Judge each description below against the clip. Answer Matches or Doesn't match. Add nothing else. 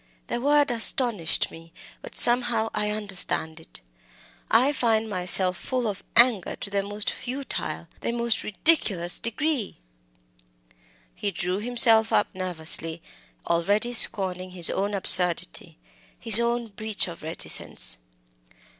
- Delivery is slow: Matches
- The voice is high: Matches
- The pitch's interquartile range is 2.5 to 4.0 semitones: Doesn't match